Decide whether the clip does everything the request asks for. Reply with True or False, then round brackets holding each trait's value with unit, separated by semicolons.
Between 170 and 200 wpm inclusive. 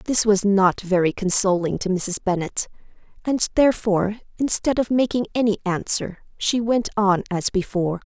False (150 wpm)